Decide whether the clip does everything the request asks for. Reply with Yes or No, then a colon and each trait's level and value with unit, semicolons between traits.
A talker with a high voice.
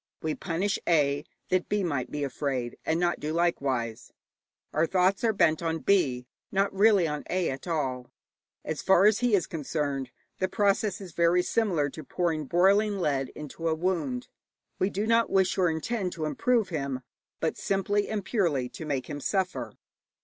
No: medium, 170 Hz